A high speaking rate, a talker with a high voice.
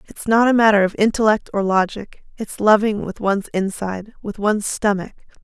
No: average, 175 wpm; high, 205 Hz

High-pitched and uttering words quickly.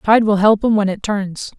Yes: high, 205 Hz; fast, 265 wpm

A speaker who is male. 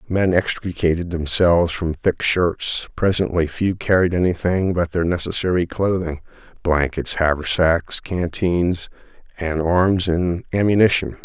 Yes: male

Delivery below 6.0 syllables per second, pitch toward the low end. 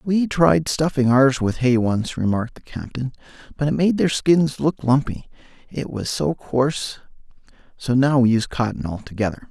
Yes: 4.9 syllables/s; low, 130 Hz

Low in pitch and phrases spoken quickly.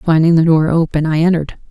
No: medium, 160 Hz; fast, 210 wpm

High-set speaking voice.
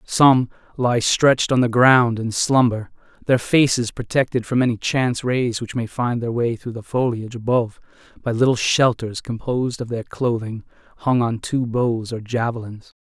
No: low, 120 Hz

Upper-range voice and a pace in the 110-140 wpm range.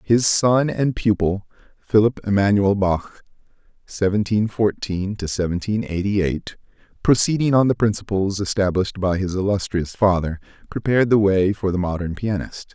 No: low, 100 Hz; slow, 135 wpm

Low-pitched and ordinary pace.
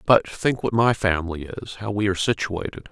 Yes: low, 100 Hz; average, 185 wpm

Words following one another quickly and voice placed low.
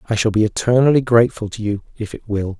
Yes: fast, 230 wpm; low, 110 Hz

